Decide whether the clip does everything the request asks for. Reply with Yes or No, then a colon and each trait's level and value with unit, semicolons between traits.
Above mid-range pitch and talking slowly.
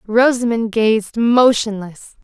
Yes: high, 225 Hz; slow, 80 wpm